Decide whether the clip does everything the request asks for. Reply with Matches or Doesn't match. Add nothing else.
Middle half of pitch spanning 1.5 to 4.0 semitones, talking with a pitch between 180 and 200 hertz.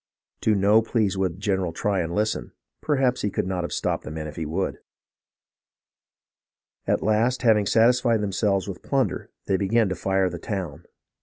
Doesn't match